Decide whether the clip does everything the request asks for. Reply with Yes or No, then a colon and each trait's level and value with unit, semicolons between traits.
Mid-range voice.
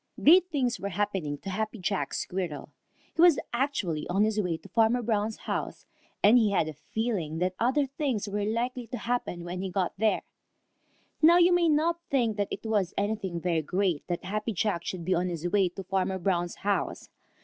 No: high, 205 Hz